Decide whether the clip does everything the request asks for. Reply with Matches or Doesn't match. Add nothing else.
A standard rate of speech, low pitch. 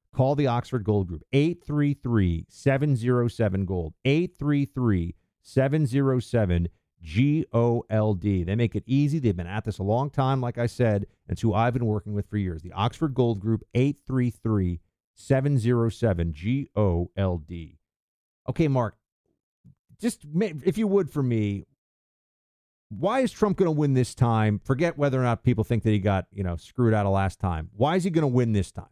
Matches